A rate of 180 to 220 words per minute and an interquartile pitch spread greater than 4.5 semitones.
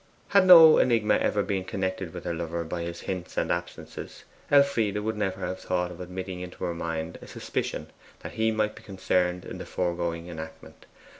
No: average, 190 wpm; average, 3.5 semitones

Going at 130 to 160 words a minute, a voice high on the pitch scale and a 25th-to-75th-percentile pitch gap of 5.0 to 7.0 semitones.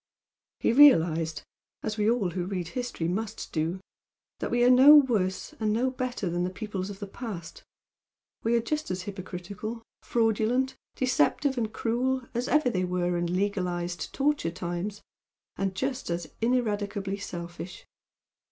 Yes: average, 150 wpm; high, 205 Hz; average, 5.3 semitones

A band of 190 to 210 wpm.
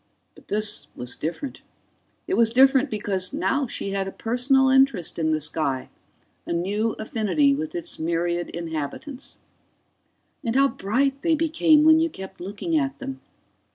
No: average, 155 wpm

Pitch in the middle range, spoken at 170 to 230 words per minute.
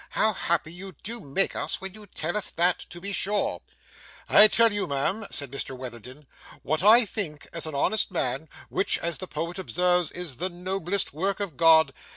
Yes: medium, 175 Hz; average, 190 wpm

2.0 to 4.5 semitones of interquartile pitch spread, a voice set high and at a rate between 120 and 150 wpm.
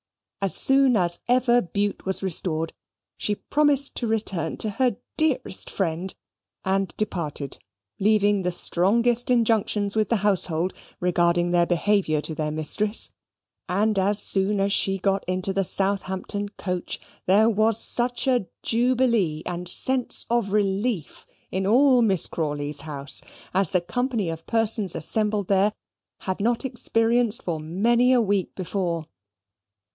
Yes: average, 4.2 semitones; high, 200 Hz; average, 140 wpm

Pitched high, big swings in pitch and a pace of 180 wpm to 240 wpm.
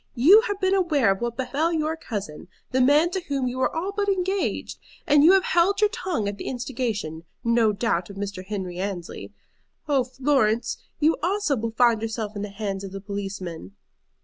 Yes: high, 245 Hz; wide, 8.2 semitones; average, 195 wpm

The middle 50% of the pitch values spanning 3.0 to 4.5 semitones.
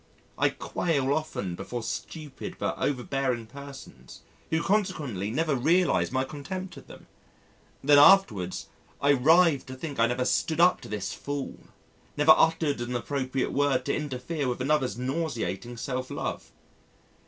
Yes: average, 3.8 semitones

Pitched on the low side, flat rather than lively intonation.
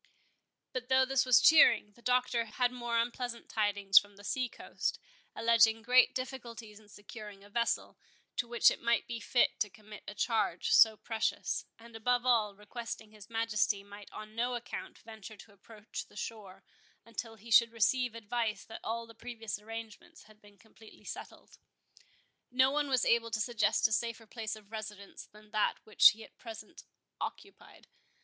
No: high, 225 Hz; narrow, 2.1 semitones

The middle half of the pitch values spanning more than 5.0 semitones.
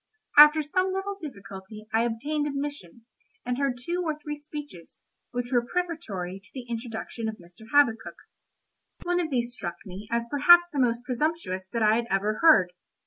Yes: wide, 5.6 semitones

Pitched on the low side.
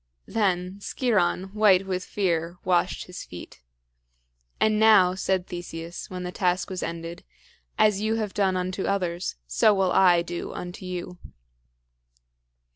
No: medium, 185 Hz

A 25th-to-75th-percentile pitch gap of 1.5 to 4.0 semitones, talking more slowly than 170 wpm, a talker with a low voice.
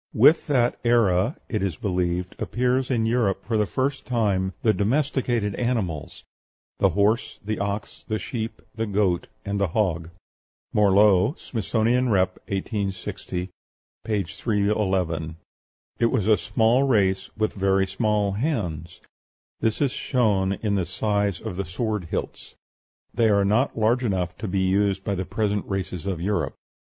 Yes: average, 3.1 semitones; average, 145 wpm; low, 105 Hz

